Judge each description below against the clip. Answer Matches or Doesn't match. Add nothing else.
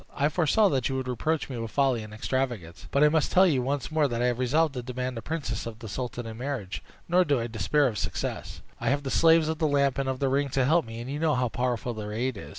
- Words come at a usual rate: Doesn't match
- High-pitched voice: Doesn't match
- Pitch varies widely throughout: Doesn't match